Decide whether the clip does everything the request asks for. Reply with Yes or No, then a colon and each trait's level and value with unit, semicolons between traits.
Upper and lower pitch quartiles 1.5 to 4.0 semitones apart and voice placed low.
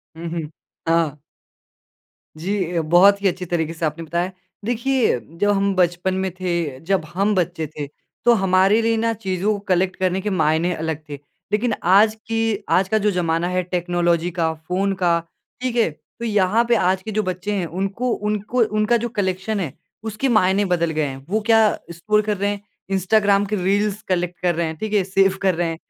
No: average, 3.5 semitones; high, 190 Hz